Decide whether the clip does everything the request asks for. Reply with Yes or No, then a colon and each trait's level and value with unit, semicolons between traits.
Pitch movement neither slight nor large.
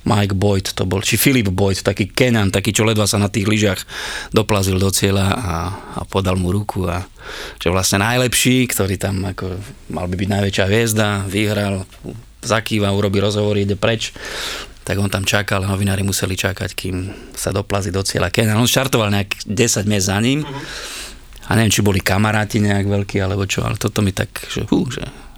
No: narrow, 2.0 semitones